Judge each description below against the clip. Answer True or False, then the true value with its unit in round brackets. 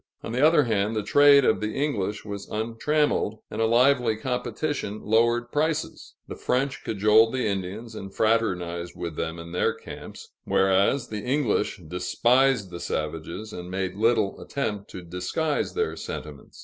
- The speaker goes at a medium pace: True (155 wpm)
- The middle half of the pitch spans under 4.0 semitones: False (4.7 semitones)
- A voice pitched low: True (110 Hz)